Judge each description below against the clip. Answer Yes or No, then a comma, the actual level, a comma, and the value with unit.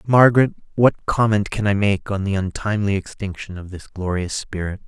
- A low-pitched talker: Yes, low, 100 Hz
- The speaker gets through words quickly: No, average, 170 wpm